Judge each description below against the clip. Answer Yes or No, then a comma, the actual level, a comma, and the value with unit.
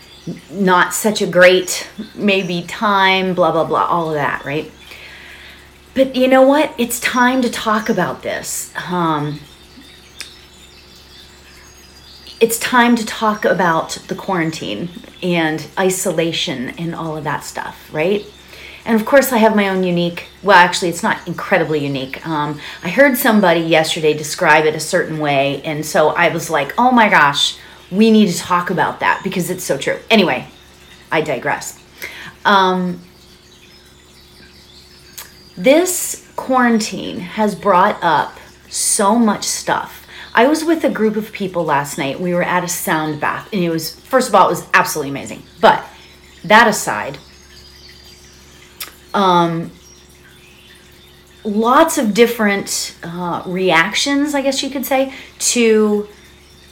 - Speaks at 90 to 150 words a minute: Yes, average, 140 wpm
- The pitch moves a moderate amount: No, wide, 8.0 semitones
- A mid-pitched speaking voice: Yes, medium, 175 Hz